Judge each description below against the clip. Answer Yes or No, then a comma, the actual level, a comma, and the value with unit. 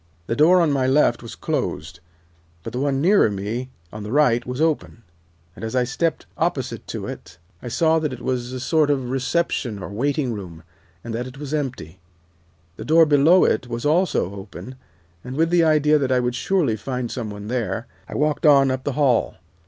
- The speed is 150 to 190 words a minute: No, average, 200 wpm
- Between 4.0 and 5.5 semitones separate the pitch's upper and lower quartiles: Yes, average, 4.4 semitones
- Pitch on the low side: Yes, low, 130 Hz